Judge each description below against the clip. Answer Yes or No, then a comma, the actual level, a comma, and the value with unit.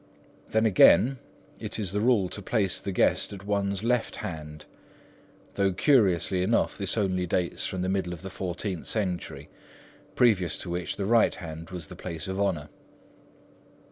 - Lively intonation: No, average, 2.7 semitones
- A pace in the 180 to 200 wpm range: No, average, 165 wpm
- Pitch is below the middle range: Yes, very low, 95 Hz